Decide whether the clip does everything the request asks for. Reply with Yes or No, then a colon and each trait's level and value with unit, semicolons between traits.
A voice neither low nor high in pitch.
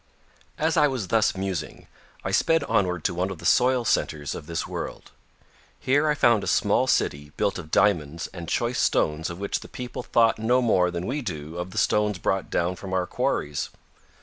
No: very low, 95 Hz